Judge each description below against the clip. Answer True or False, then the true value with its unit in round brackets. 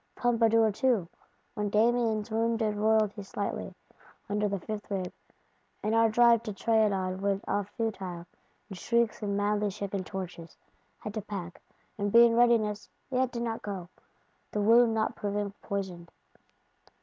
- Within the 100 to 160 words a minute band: True (140 wpm)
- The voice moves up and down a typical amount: False (2.2 semitones)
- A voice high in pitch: True (210 Hz)